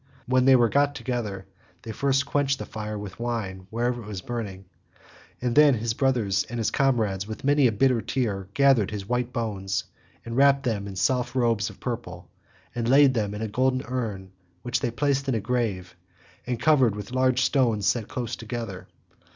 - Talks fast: No, average, 185 wpm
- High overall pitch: No, low, 120 Hz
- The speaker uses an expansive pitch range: No, average, 3.8 semitones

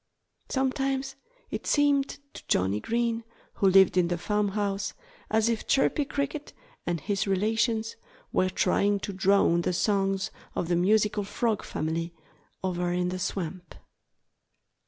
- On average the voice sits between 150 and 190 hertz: No, high, 200 Hz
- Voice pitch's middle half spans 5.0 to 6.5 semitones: No, average, 4.2 semitones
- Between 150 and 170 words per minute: No, slow, 135 wpm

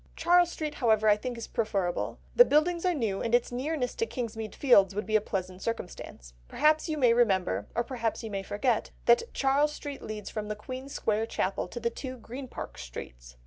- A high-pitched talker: Yes, high, 230 Hz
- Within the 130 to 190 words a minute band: No, fast, 205 wpm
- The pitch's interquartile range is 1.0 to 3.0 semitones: No, average, 4.7 semitones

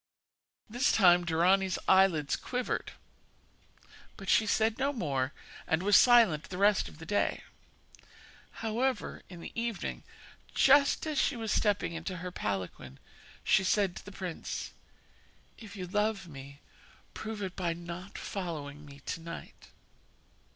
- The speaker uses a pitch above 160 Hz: Yes, high, 190 Hz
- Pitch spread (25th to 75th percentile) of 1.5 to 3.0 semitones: No, average, 4.6 semitones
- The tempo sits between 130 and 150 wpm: Yes, slow, 135 wpm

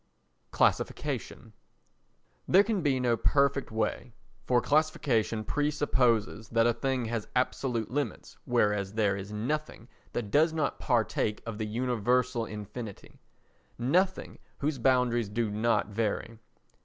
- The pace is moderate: No, slow, 120 wpm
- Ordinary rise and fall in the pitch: Yes, average, 3.6 semitones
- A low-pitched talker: Yes, low, 120 Hz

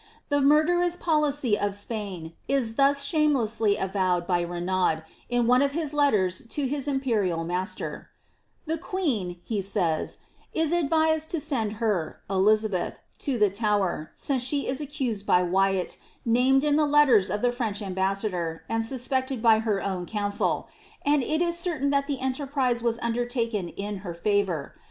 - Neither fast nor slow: Yes, average, 160 wpm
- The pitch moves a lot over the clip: Yes, wide, 6.3 semitones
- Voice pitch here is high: Yes, high, 230 Hz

